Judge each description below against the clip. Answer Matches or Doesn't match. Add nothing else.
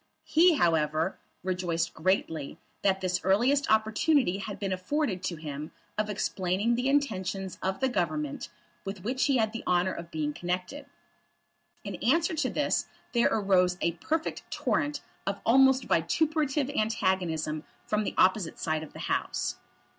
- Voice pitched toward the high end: Matches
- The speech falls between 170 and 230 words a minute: Doesn't match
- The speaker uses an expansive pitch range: Matches